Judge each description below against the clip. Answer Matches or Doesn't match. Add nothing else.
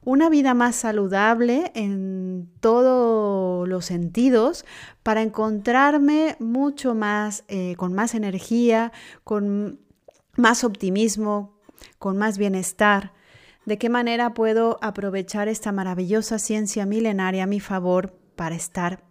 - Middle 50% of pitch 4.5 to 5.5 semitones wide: Doesn't match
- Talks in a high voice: Matches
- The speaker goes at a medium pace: Doesn't match